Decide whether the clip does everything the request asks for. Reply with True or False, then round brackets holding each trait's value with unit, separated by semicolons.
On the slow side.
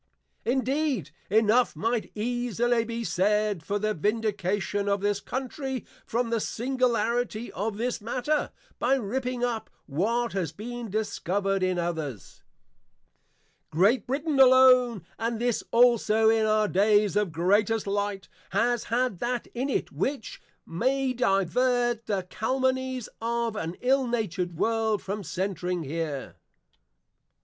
True (125 wpm)